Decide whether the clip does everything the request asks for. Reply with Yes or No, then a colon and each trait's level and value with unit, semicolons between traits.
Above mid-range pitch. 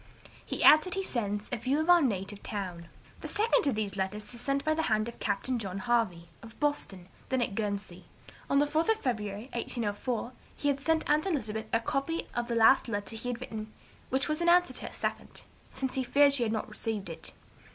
Yes: high, 240 Hz